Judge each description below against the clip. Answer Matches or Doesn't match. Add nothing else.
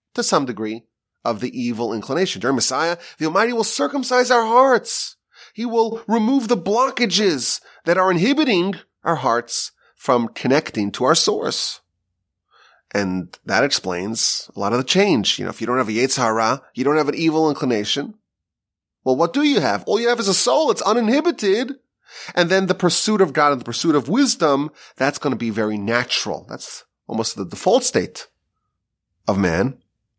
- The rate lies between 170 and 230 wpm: Matches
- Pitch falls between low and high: Matches